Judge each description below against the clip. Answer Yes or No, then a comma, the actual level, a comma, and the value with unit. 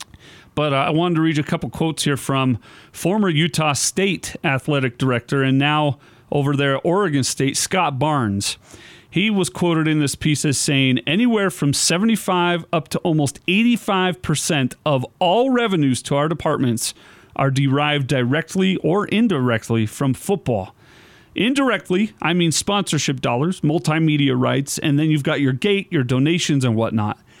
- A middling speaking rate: Yes, average, 155 wpm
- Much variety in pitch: No, average, 4.4 semitones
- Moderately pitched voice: Yes, medium, 150 Hz